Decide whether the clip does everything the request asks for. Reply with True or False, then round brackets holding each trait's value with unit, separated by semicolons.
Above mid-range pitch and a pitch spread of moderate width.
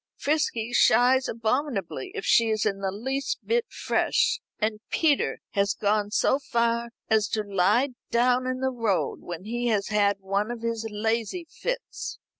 True (230 Hz; 3.7 semitones)